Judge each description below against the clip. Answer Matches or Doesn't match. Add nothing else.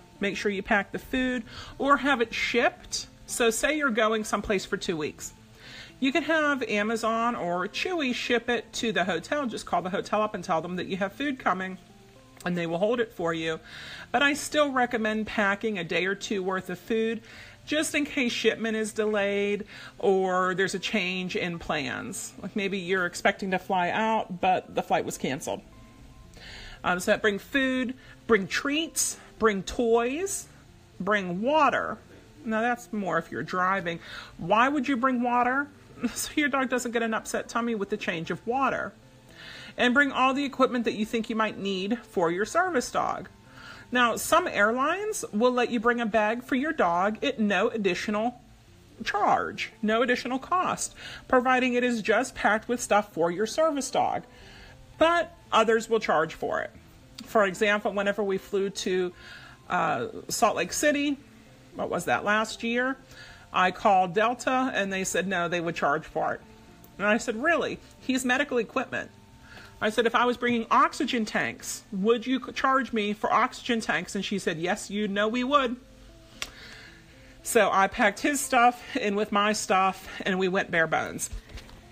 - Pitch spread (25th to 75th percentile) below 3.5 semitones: Doesn't match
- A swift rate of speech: Doesn't match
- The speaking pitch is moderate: Doesn't match